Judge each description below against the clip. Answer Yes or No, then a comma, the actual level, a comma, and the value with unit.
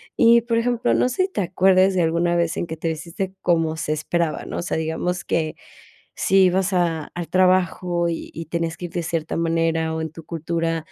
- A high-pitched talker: No, medium, 170 Hz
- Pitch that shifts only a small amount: Yes, narrow, 2.1 semitones